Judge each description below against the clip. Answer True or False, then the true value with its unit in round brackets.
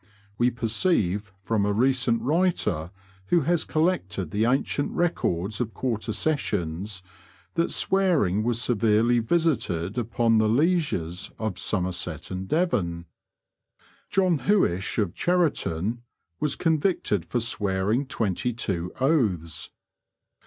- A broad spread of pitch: True (7.9 semitones)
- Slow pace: True (110 wpm)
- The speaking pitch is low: True (115 Hz)